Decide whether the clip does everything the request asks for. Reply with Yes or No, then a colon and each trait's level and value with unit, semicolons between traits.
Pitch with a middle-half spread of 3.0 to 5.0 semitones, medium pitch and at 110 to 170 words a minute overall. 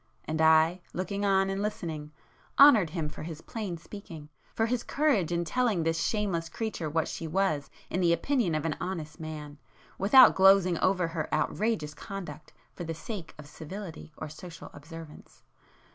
Yes: average, 3.9 semitones; medium, 170 Hz; average, 165 wpm